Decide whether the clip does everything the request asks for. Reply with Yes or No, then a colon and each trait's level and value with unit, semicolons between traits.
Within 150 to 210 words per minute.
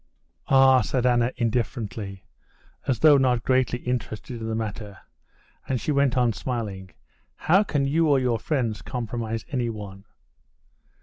No: slow, 135 wpm